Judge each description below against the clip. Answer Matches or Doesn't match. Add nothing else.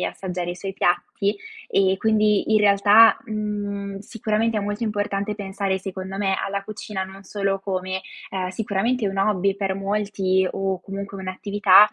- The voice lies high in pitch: Matches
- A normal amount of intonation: Doesn't match